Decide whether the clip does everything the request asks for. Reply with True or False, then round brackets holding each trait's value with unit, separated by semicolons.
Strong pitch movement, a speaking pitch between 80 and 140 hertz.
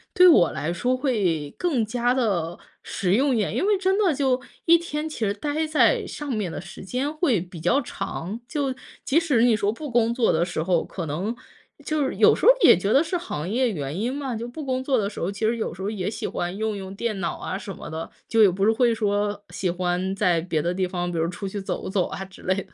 False (6.1 semitones; 215 Hz)